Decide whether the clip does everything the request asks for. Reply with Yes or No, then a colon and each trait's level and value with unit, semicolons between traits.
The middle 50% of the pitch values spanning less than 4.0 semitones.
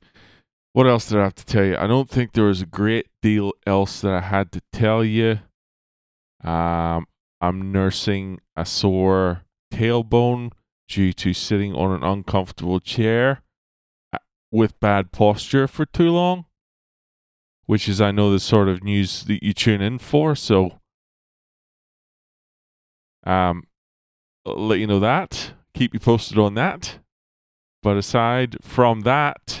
Yes: average, 3.6 semitones